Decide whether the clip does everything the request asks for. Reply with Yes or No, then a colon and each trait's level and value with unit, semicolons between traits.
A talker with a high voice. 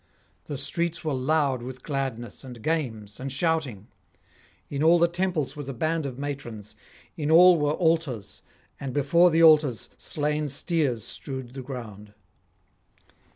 No: medium, 140 Hz